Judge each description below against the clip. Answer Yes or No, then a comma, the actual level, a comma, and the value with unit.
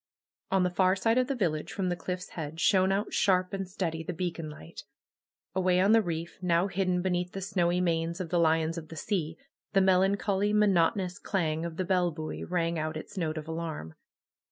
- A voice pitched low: No, medium, 180 Hz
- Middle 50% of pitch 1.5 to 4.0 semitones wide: Yes, narrow, 2.6 semitones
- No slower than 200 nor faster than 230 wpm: Yes, fast, 205 wpm